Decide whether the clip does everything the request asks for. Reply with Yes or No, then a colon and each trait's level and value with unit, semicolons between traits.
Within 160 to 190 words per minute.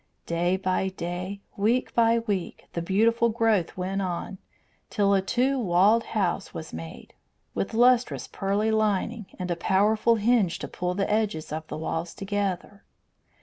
No: average, 150 wpm